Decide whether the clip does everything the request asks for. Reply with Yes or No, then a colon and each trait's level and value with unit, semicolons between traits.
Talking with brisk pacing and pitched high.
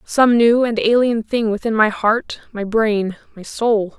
No: average, 180 wpm; high, 225 Hz